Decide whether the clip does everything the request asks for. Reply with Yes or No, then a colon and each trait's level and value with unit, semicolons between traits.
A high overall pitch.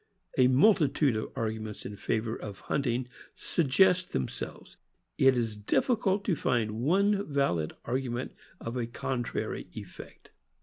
No: low, 125 Hz